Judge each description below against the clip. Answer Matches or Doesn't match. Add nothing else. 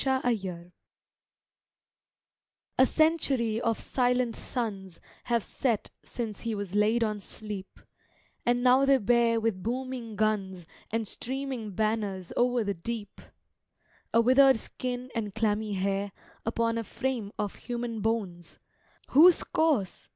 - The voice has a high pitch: Matches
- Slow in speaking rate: Matches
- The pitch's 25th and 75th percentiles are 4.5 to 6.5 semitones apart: Doesn't match